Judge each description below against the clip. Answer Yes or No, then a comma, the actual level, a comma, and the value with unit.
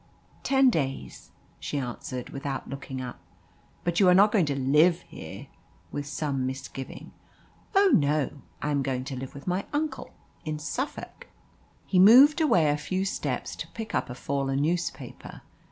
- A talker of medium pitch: Yes, medium, 150 Hz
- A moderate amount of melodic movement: No, wide, 5.9 semitones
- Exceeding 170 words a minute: No, average, 160 wpm